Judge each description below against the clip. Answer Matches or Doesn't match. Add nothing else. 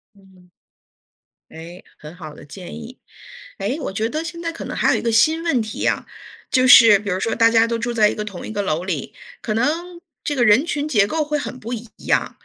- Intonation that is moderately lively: Doesn't match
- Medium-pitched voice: Doesn't match